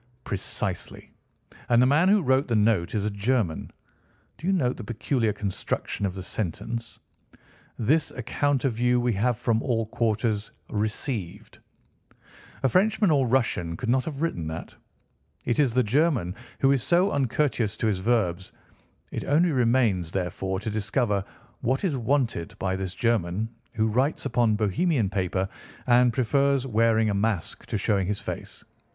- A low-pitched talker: Yes, low, 115 Hz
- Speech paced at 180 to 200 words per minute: No, average, 155 wpm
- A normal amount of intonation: Yes, average, 4.5 semitones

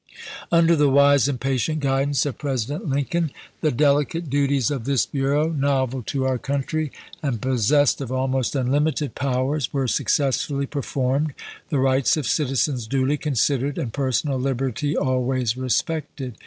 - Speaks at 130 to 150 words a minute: Yes, average, 145 wpm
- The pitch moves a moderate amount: No, narrow, 1.9 semitones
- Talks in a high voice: No, low, 135 Hz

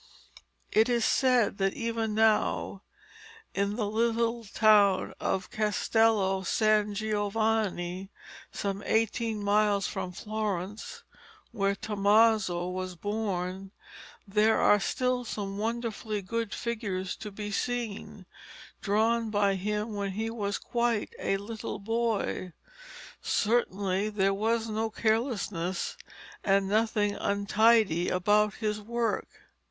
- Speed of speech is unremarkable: No, slow, 110 wpm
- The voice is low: No, high, 210 Hz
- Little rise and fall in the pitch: Yes, narrow, 2.2 semitones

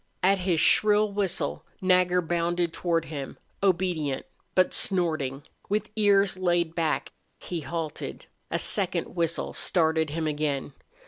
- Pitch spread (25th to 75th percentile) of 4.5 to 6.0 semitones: No, average, 2.7 semitones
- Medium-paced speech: No, slow, 125 wpm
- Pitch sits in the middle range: Yes, medium, 170 Hz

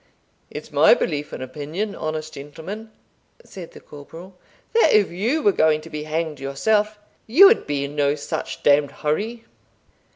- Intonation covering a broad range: Yes, wide, 6.2 semitones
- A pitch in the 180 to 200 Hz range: No, medium, 160 Hz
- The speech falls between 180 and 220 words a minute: No, average, 165 wpm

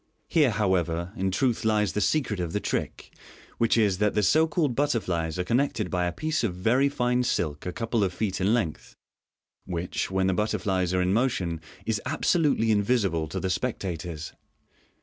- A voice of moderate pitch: No, low, 105 Hz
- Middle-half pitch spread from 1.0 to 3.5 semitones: No, average, 4.9 semitones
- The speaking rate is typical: Yes, average, 180 wpm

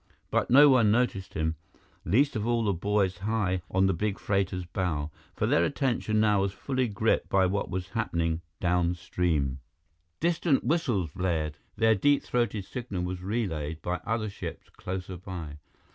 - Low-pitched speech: Yes, very low, 95 Hz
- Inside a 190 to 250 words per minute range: No, average, 160 wpm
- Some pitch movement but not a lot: Yes, average, 4.1 semitones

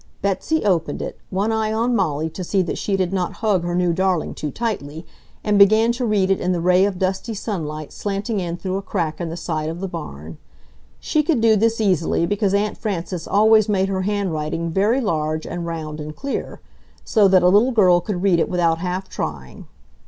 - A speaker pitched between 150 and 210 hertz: Yes, high, 190 Hz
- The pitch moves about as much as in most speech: Yes, average, 3.8 semitones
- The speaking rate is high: Yes, fast, 210 wpm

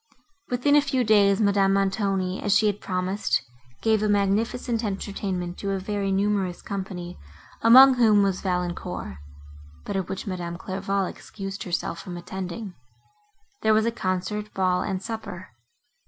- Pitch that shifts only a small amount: Yes, narrow, 2.3 semitones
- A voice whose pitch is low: No, high, 195 Hz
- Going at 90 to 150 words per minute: Yes, average, 145 wpm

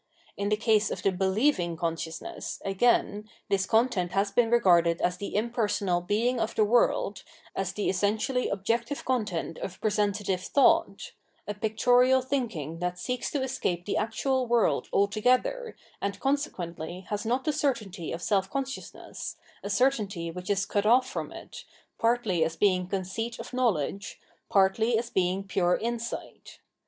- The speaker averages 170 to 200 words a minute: No, average, 155 wpm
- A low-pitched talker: No, high, 210 Hz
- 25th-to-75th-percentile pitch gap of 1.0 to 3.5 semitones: No, average, 4.4 semitones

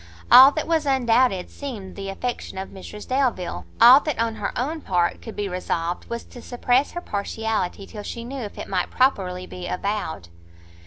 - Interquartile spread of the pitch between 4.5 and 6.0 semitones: Yes, average, 5.1 semitones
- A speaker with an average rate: Yes, average, 180 wpm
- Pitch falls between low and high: No, high, 225 Hz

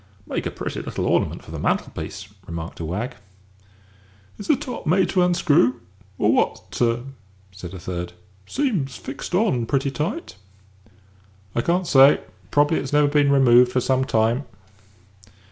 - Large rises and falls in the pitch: Yes, wide, 5.9 semitones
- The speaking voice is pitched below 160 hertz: Yes, low, 135 Hz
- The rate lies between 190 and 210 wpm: No, average, 155 wpm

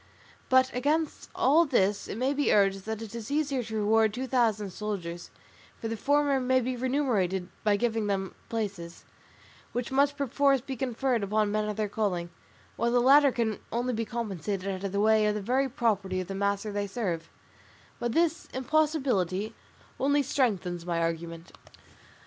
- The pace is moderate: Yes, average, 165 wpm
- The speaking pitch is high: Yes, high, 220 Hz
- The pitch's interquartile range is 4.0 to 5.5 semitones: Yes, average, 4.7 semitones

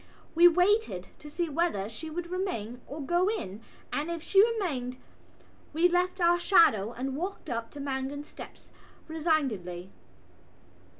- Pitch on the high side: Yes, very high, 315 Hz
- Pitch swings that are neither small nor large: No, wide, 5.9 semitones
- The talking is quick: No, average, 140 wpm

